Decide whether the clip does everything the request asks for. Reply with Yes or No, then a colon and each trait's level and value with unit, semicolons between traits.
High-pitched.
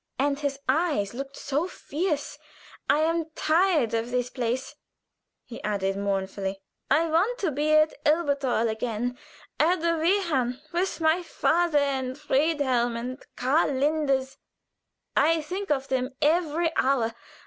Yes: very high, 285 Hz